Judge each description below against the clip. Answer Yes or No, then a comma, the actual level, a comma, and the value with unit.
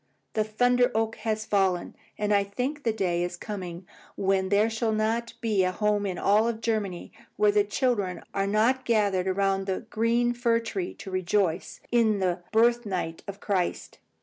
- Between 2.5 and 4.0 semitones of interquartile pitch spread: Yes, average, 3.2 semitones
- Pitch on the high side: Yes, high, 210 Hz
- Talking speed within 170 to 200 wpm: Yes, average, 175 wpm